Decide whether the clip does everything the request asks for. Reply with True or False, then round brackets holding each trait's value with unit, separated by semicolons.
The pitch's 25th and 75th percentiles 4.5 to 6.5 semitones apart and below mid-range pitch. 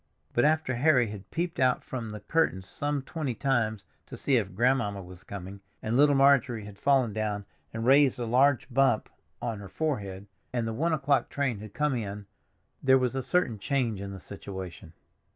True (5.2 semitones; 120 Hz)